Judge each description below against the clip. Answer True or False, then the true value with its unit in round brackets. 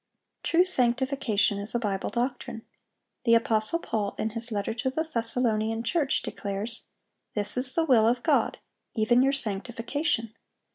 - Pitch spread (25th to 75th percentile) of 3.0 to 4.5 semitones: True (3.3 semitones)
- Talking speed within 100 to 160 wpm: True (145 wpm)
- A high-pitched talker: True (230 Hz)